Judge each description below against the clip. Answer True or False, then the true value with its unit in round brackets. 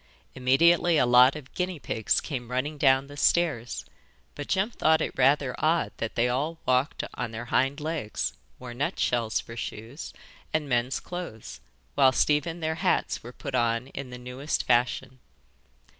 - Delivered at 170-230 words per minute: False (160 wpm)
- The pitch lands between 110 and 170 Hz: True (135 Hz)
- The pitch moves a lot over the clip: False (4.0 semitones)